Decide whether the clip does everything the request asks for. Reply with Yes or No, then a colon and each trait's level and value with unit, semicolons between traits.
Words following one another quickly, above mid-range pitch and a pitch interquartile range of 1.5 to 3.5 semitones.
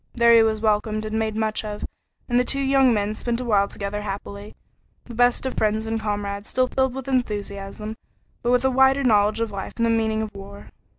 Yes: fast, 220 wpm; high, 220 Hz; average, 2.8 semitones